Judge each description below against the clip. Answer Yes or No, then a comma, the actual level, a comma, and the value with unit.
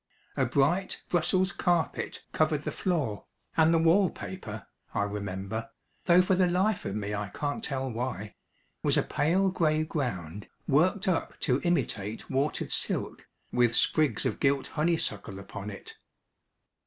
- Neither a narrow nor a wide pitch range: No, wide, 8.5 semitones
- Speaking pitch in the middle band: Yes, medium, 145 Hz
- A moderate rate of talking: Yes, average, 145 wpm